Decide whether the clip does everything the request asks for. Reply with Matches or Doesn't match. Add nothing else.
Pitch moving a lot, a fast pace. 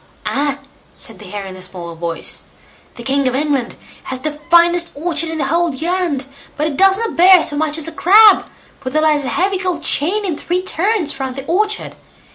Doesn't match